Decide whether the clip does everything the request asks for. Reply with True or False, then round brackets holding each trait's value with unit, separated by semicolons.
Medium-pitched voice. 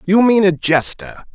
True (175 Hz)